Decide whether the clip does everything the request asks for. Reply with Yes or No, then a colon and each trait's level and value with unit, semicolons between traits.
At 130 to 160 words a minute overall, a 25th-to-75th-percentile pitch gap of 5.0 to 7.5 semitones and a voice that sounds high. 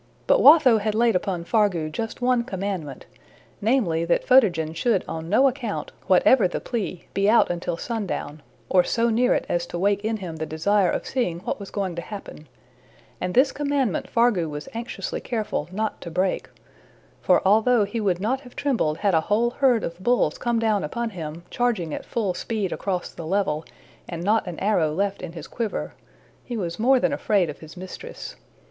No: average, 190 wpm; average, 5.3 semitones; high, 200 Hz